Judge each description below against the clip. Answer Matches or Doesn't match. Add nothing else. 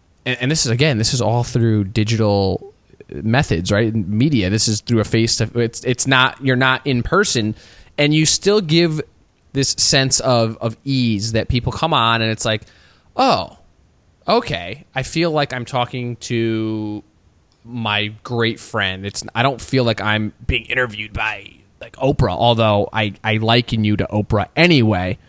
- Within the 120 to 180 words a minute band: Matches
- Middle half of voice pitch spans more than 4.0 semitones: Doesn't match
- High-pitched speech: Doesn't match